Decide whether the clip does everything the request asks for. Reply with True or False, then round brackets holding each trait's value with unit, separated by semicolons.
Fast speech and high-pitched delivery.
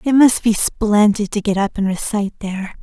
True (210 wpm; 210 Hz)